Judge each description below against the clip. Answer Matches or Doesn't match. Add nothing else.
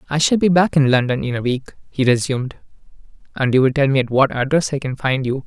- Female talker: Doesn't match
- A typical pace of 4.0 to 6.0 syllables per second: Doesn't match